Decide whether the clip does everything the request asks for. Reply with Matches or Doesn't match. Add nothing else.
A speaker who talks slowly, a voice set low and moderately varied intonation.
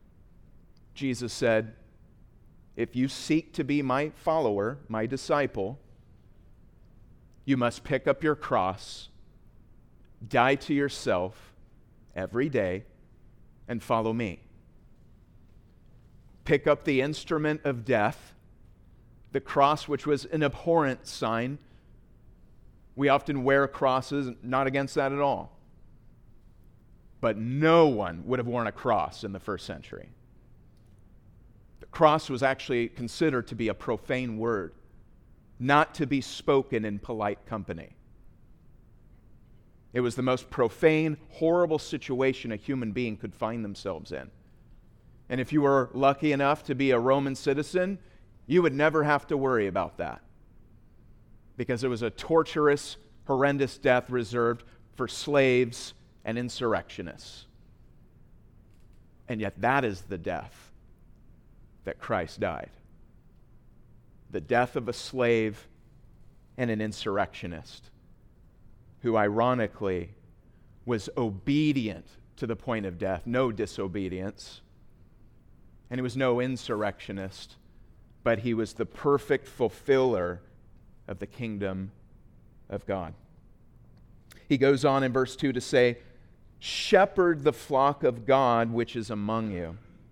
Matches